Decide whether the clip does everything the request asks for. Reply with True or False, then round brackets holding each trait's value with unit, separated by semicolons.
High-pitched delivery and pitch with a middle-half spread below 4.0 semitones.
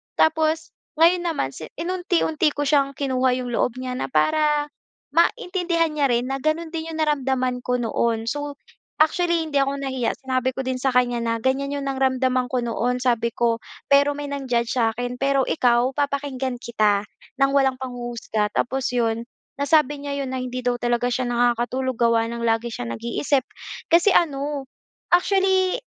True (265 Hz; 3.3 semitones)